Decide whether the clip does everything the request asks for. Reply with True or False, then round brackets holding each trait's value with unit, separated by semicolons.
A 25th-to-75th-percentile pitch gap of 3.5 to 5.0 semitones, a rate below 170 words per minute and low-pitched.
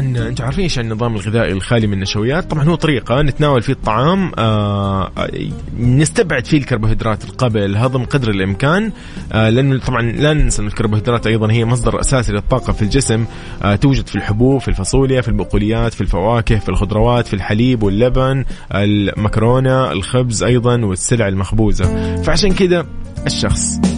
True (4.0 semitones; 140 wpm; 115 Hz)